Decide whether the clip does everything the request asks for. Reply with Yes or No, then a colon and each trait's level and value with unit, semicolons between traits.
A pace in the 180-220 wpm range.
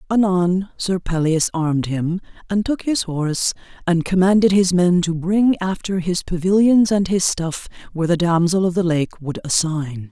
No: average, 170 wpm